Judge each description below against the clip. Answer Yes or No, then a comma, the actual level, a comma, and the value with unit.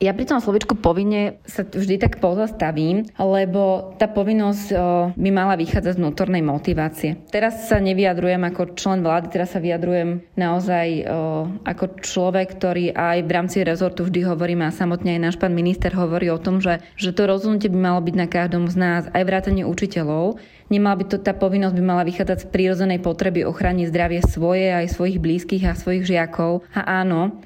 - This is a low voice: No, medium, 180 Hz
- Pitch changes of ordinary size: No, narrow, 2.0 semitones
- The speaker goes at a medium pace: No, fast, 185 wpm